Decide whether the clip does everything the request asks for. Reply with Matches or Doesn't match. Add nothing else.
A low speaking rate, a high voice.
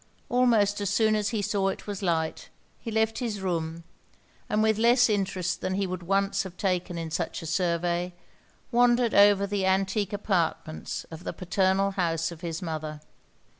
Doesn't match